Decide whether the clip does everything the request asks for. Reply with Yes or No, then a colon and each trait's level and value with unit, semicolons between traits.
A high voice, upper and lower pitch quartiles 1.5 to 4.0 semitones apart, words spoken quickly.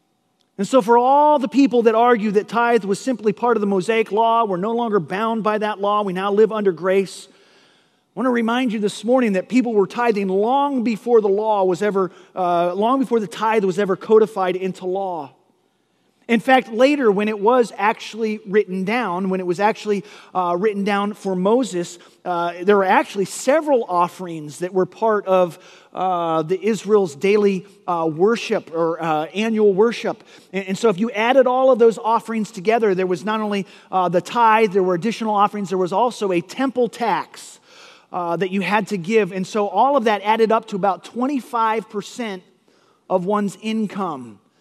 No: high, 210 Hz; average, 3.3 semitones; average, 190 wpm